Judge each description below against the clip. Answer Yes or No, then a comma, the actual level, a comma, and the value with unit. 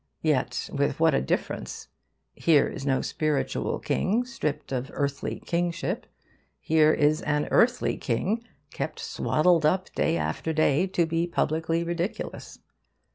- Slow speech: Yes, slow, 130 wpm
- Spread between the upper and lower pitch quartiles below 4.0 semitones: Yes, average, 3.2 semitones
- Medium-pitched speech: Yes, medium, 160 Hz